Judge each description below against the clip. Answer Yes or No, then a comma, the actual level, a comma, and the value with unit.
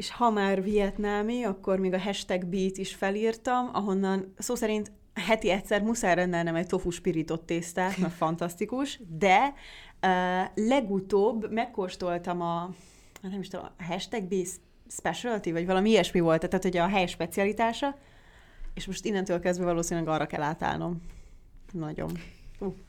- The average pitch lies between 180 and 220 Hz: Yes, high, 190 Hz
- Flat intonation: No, average, 3.1 semitones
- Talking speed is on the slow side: No, average, 145 wpm